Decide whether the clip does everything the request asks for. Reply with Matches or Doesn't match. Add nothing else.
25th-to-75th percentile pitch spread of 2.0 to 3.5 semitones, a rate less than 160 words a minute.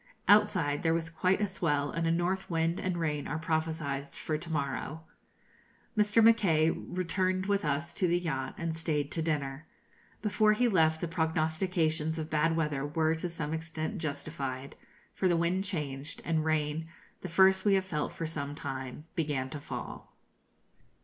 Doesn't match